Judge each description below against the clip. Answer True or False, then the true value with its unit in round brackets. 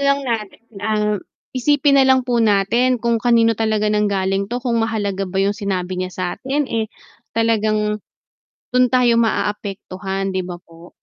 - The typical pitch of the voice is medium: False (215 Hz)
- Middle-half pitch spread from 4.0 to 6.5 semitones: False (3.3 semitones)